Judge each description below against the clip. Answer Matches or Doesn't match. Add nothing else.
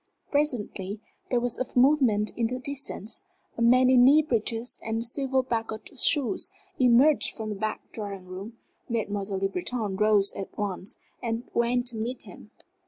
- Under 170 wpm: Matches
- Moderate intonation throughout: Matches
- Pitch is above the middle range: Matches